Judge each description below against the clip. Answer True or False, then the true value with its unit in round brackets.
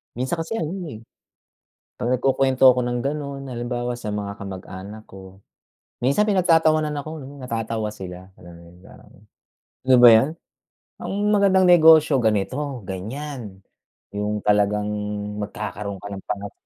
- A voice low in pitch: True (120 Hz)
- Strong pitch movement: True (5.8 semitones)